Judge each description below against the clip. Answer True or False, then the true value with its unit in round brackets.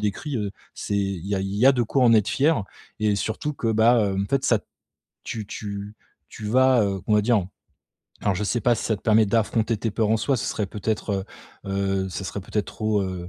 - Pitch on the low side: True (105 Hz)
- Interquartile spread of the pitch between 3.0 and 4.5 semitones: False (2.5 semitones)